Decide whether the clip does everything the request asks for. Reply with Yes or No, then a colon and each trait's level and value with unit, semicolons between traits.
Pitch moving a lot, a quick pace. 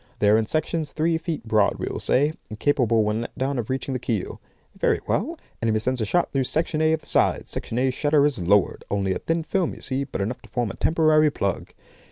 Yes: wide, 6.0 semitones; fast, 245 wpm